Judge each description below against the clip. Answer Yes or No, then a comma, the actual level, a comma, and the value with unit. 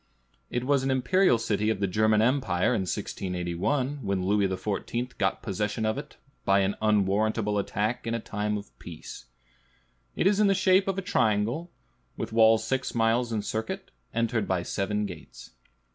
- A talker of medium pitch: No, low, 110 Hz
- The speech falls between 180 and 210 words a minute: No, average, 160 wpm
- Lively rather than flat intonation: No, average, 3.8 semitones